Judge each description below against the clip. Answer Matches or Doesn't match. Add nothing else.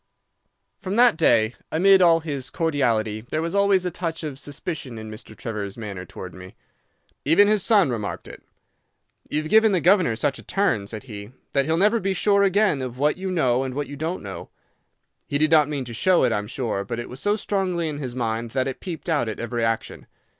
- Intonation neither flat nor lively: Doesn't match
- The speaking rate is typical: Doesn't match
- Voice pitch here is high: Doesn't match